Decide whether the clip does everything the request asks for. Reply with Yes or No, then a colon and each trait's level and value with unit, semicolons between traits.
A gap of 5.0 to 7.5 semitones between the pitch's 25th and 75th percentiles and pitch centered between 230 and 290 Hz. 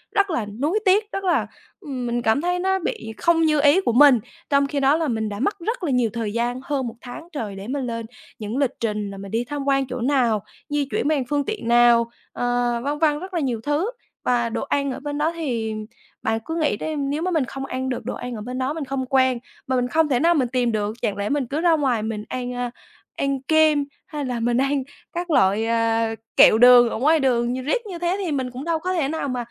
No: average, 4.3 semitones; very high, 265 Hz